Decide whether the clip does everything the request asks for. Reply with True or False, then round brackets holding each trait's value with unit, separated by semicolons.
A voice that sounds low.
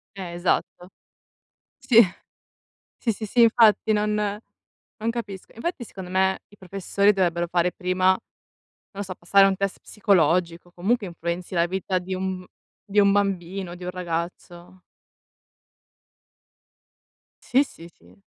False (190 Hz)